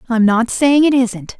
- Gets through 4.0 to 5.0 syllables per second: Yes, 4.1 syllables/s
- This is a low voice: No, high, 240 Hz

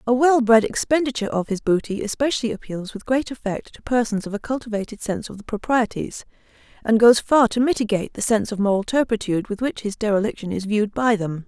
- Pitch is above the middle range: Yes, high, 225 Hz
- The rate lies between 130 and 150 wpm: No, fast, 205 wpm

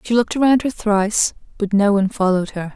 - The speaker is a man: No, female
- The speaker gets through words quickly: Yes, fast, 215 wpm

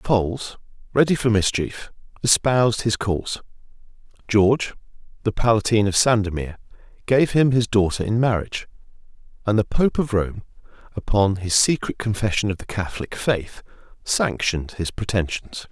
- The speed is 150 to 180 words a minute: No, slow, 135 wpm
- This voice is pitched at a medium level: No, low, 110 Hz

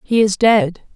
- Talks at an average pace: Yes, average, 190 wpm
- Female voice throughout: Yes, female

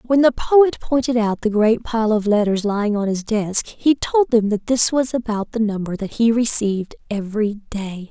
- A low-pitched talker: No, high, 225 Hz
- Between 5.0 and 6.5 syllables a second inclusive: No, 4.7 syllables/s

